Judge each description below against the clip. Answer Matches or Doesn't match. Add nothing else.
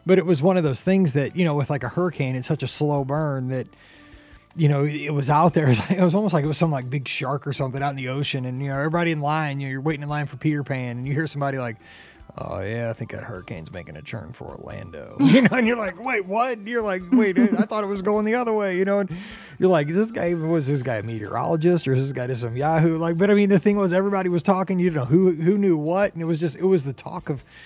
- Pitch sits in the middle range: Matches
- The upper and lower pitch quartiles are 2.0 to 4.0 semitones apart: Doesn't match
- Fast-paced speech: Matches